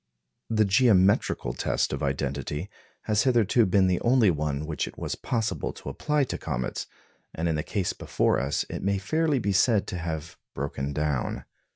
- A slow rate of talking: No, average, 175 wpm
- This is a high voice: No, very low, 90 Hz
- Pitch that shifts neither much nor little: No, wide, 6.8 semitones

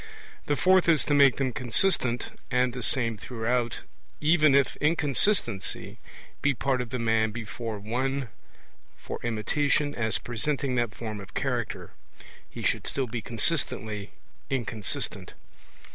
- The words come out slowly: Yes, slow, 130 wpm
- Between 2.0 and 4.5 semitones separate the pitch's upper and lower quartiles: Yes, average, 3.8 semitones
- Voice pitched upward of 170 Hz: No, low, 125 Hz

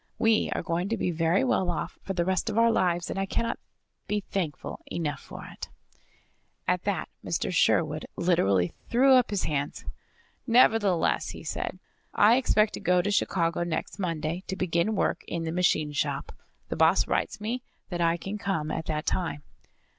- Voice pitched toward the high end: No, medium, 180 Hz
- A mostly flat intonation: No, average, 3.9 semitones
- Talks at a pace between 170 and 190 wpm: Yes, average, 180 wpm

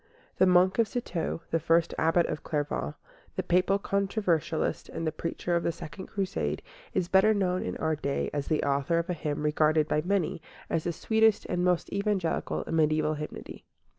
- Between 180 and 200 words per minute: Yes, average, 185 wpm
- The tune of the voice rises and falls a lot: No, average, 3.5 semitones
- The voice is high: No, medium, 170 Hz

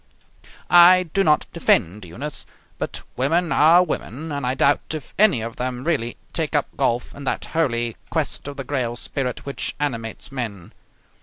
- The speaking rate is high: No, average, 165 wpm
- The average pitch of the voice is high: No, low, 135 Hz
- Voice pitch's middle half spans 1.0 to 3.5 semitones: No, average, 4.7 semitones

